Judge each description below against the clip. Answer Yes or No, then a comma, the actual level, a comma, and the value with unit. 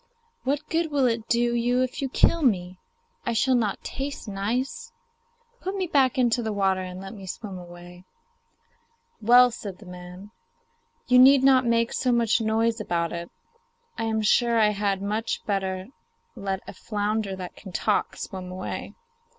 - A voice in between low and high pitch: No, high, 220 Hz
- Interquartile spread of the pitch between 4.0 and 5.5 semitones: Yes, average, 4.5 semitones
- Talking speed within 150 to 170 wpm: Yes, average, 165 wpm